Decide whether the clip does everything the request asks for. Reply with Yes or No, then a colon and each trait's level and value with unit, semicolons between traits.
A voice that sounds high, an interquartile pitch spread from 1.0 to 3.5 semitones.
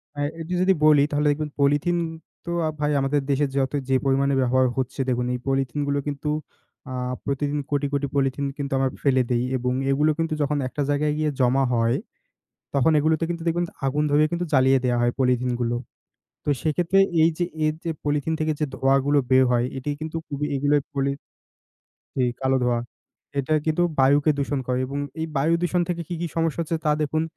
No: medium, 145 Hz; narrow, 2.6 semitones